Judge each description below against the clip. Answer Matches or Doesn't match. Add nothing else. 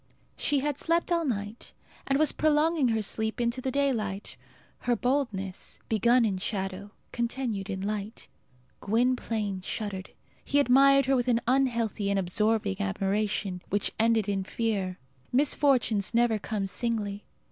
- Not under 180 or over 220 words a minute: Doesn't match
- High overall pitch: Matches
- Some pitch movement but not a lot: Matches